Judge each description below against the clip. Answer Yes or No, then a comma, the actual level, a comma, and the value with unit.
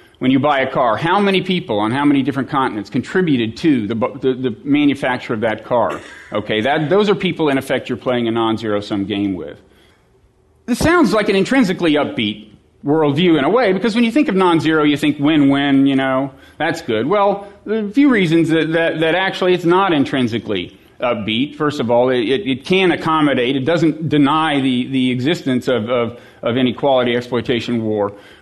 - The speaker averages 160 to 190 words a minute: No, average, 200 wpm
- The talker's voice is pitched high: No, medium, 140 Hz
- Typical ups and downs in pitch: No, wide, 6.4 semitones